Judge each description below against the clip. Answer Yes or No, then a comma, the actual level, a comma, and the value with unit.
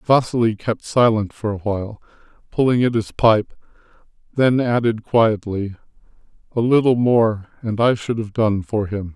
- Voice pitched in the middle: No, low, 110 Hz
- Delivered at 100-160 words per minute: Yes, average, 150 wpm